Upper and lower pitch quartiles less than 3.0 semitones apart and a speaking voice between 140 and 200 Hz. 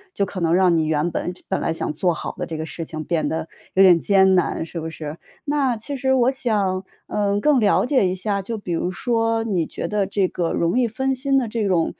No: average, 5.1 semitones; high, 195 Hz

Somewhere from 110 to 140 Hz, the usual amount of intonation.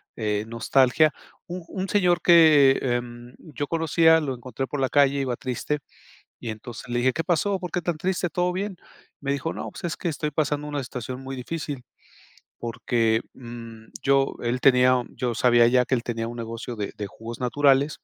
Yes: low, 135 Hz; average, 4.5 semitones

